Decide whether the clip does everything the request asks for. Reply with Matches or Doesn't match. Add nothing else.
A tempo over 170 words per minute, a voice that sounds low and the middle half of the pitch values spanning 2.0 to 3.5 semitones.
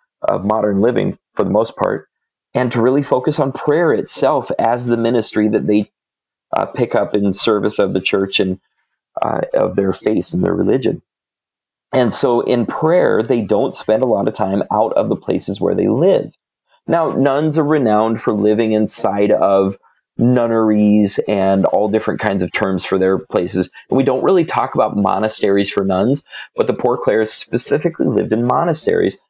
Matches